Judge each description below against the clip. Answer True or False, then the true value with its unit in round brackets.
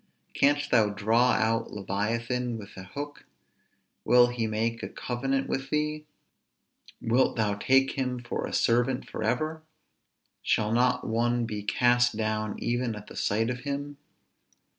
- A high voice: False (120 Hz)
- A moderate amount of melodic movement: True (3.0 semitones)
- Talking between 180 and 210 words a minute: False (140 wpm)